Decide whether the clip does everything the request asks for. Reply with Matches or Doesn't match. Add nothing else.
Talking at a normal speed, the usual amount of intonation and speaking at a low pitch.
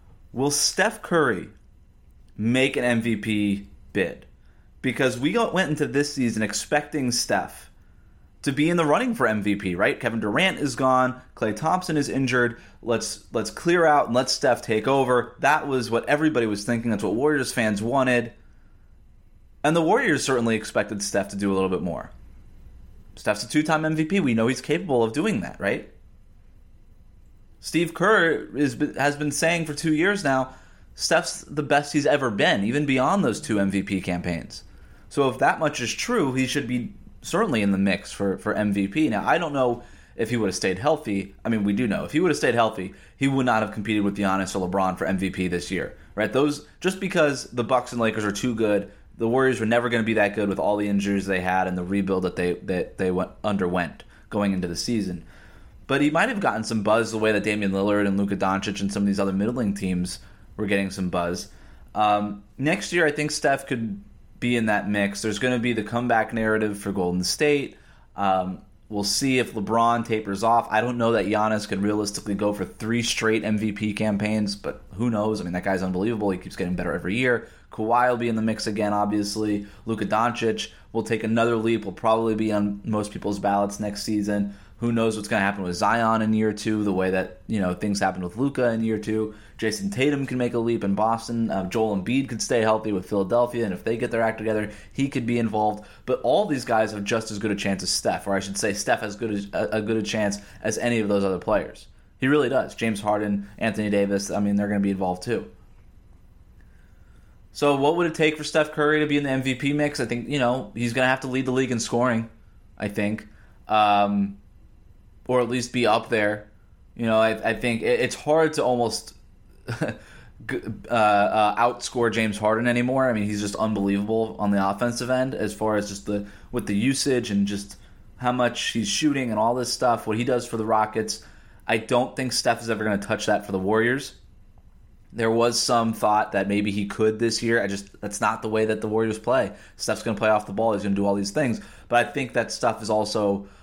Doesn't match